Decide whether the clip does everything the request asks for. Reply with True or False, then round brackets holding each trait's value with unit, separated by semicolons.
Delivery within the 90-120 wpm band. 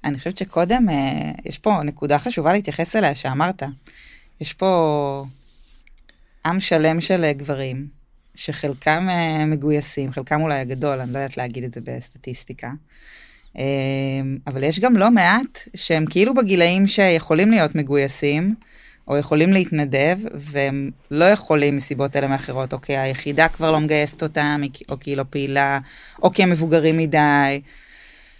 False (145 wpm)